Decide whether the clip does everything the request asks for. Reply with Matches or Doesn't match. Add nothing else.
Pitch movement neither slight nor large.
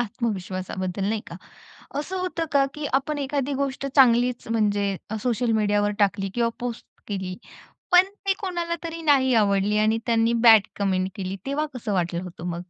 Doesn't match